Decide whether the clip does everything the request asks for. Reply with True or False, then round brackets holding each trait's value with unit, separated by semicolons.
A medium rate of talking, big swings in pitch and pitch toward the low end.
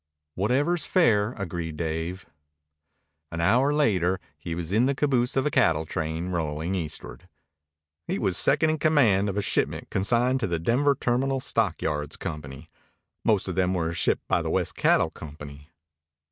True (160 wpm; 7.3 semitones; 95 Hz)